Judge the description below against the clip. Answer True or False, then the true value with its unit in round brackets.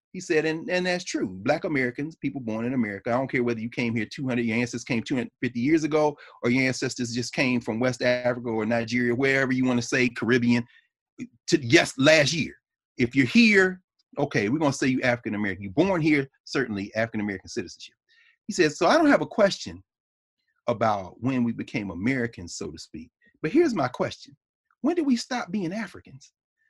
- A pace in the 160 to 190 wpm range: False (200 wpm)